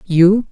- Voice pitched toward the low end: No, high, 190 Hz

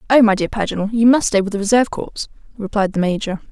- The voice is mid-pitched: No, high, 210 Hz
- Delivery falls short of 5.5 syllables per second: No, 6.8 syllables/s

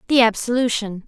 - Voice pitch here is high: Yes, high, 230 Hz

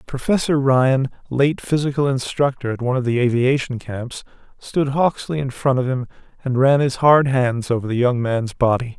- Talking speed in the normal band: Yes, average, 180 wpm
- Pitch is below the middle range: Yes, low, 130 Hz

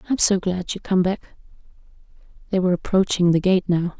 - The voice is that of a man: No, female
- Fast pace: No, average, 180 wpm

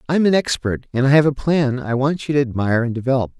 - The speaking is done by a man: Yes, male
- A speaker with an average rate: No, fast, 280 wpm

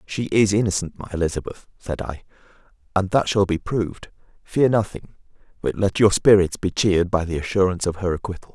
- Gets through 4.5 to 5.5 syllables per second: No, 5.9 syllables/s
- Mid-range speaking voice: No, very low, 95 Hz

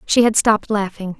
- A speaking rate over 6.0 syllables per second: No, 5.6 syllables/s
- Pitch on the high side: Yes, high, 210 Hz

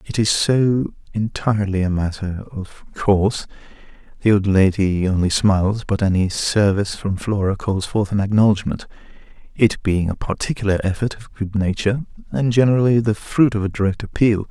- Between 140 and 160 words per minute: Yes, average, 155 wpm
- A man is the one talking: Yes, male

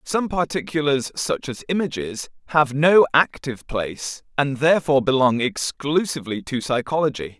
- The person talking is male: Yes, male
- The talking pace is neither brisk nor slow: No, slow, 120 wpm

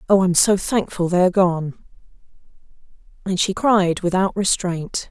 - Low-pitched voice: No, medium, 185 Hz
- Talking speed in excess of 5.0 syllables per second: No, 4.9 syllables/s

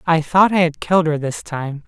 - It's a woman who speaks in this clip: No, male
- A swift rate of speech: Yes, fast, 255 wpm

